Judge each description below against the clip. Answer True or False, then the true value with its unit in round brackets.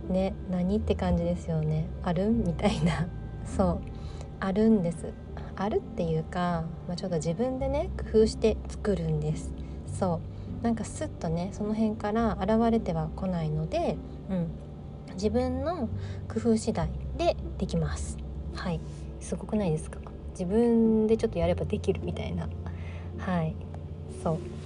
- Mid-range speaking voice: True (155 Hz)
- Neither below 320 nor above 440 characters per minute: False (285 characters per minute)